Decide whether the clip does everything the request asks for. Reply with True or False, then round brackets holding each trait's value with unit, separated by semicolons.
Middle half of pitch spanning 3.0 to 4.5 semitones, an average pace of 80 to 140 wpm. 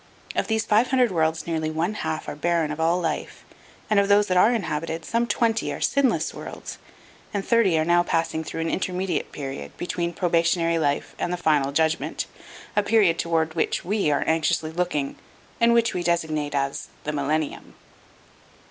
False (3.9 semitones; 180 wpm)